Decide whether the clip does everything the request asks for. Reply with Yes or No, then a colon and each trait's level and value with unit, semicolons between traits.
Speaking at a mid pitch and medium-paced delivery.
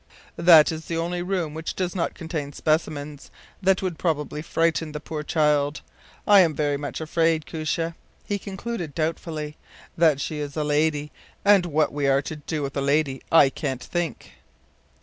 Yes: medium, 155 Hz; average, 170 wpm